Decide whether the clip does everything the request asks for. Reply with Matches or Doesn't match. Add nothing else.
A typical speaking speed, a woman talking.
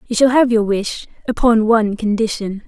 Matches